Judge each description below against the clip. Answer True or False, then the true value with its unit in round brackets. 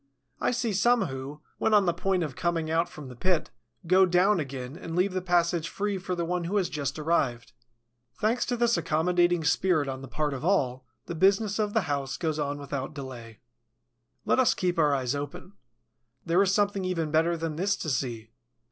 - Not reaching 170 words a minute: False (200 wpm)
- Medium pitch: True (170 Hz)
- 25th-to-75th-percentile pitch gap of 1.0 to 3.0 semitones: False (4.9 semitones)